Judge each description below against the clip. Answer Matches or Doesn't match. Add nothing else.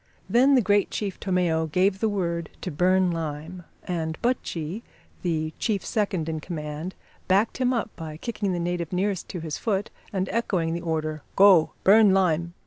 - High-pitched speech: Doesn't match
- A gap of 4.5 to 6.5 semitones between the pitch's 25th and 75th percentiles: Doesn't match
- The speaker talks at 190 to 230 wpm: Doesn't match